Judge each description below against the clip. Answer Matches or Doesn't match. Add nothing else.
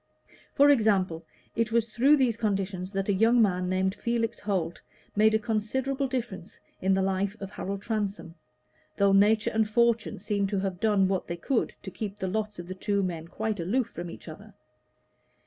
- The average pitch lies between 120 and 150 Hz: Doesn't match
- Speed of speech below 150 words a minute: Doesn't match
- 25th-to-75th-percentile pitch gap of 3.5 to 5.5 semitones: Doesn't match